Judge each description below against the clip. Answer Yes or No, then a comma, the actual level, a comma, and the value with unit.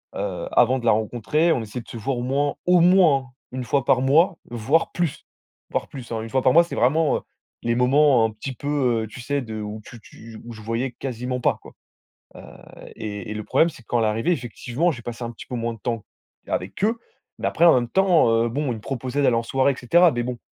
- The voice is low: Yes, low, 125 Hz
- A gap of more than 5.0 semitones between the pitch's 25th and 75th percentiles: No, average, 3.8 semitones